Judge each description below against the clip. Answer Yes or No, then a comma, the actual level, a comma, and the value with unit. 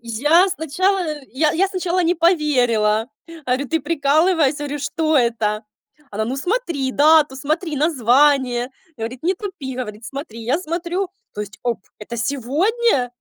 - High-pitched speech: Yes, very high, 285 Hz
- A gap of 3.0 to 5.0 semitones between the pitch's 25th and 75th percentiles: No, wide, 5.6 semitones